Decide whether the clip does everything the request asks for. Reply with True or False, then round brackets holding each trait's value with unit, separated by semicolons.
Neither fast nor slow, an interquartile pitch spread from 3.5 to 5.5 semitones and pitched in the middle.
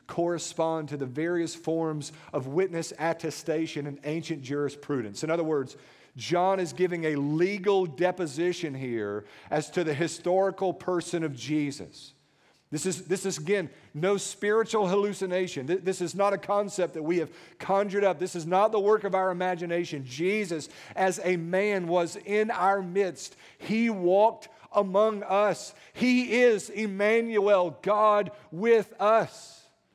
True (145 wpm; 4.0 semitones; 180 Hz)